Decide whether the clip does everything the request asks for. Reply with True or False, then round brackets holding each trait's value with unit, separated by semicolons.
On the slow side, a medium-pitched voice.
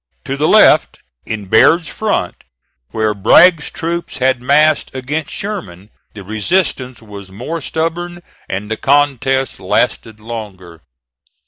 False (120 wpm; 130 Hz)